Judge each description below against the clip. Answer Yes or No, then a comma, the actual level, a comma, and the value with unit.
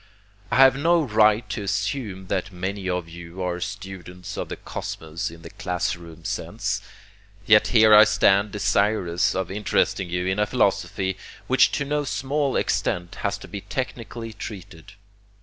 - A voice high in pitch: No, low, 100 Hz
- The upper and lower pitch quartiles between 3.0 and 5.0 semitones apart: Yes, average, 3.7 semitones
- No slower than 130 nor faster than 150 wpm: No, average, 160 wpm